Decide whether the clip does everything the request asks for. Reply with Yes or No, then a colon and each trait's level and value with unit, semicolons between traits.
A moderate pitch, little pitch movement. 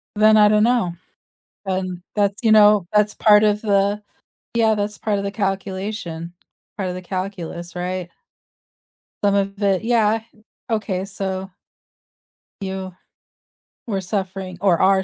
No: high, 195 Hz; narrow, 2.0 semitones